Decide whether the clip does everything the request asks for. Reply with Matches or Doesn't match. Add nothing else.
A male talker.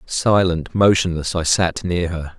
Matches